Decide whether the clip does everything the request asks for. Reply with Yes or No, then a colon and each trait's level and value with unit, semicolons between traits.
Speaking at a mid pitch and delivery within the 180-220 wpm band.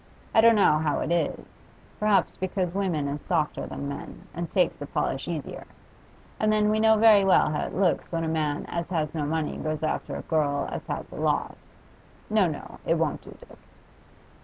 Yes: medium, 165 Hz; average, 200 wpm